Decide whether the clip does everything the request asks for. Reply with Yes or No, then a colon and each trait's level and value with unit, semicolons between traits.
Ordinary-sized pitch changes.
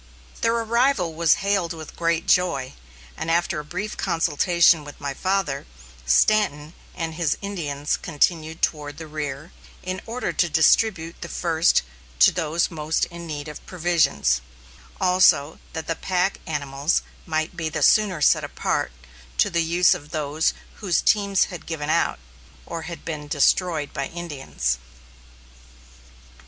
Yes: average, 3.3 semitones